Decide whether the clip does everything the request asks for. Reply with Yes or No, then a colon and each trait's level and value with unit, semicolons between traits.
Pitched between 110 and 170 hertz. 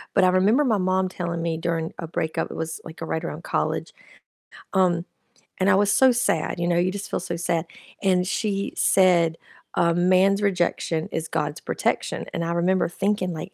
No: medium, 180 Hz